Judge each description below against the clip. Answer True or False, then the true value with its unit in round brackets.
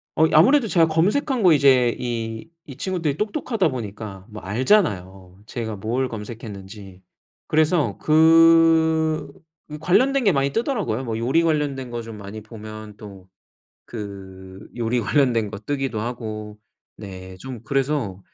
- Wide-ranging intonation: True (7.1 semitones)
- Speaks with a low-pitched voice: True (125 Hz)